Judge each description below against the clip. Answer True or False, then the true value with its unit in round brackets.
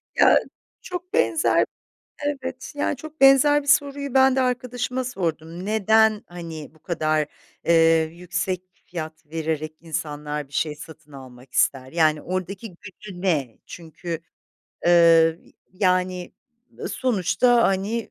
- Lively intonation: True (7.0 semitones)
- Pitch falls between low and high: True (180 Hz)